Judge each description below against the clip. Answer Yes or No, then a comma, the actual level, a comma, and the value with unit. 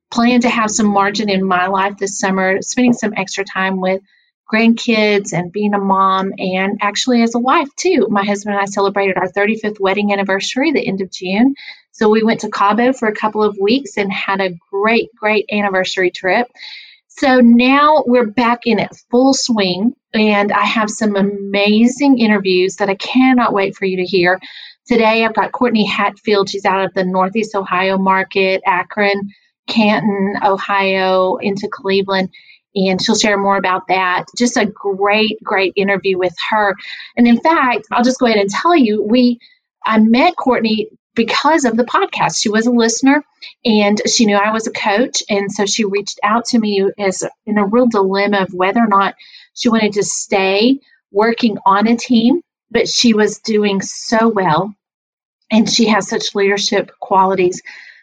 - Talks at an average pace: Yes, average, 180 wpm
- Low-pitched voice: No, high, 210 Hz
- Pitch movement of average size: Yes, average, 3.2 semitones